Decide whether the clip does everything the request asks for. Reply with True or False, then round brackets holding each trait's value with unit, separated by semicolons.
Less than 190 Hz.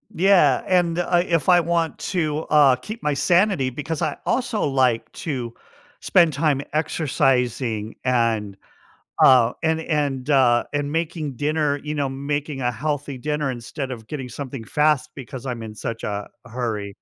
True (140 Hz)